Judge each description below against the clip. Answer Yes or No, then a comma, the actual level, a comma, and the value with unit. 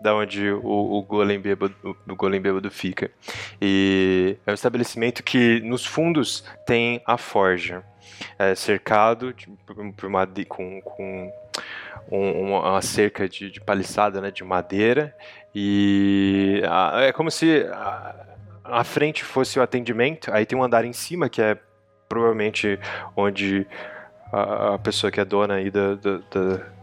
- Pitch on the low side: Yes, low, 100 Hz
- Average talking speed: Yes, average, 150 wpm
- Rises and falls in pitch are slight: No, average, 3.1 semitones